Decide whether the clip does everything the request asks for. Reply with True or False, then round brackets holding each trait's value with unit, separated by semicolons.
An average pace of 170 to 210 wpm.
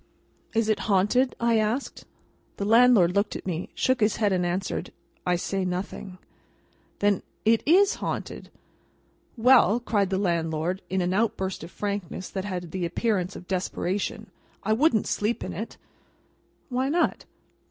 False (145 wpm)